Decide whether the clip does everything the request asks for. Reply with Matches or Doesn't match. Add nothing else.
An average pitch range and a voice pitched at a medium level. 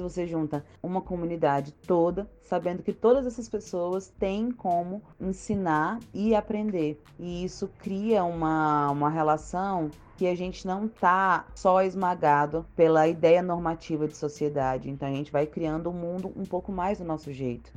Matches